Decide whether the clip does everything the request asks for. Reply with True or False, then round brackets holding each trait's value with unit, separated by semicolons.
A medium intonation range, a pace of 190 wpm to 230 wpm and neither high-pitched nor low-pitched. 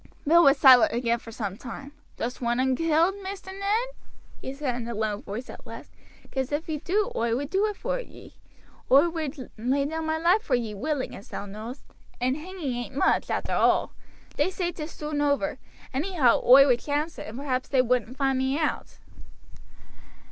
False (4.7 semitones; 195 wpm; 275 Hz)